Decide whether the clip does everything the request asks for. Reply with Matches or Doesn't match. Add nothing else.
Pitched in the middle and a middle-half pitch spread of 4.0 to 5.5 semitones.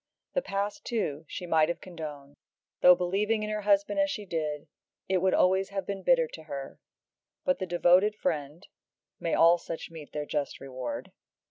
Matches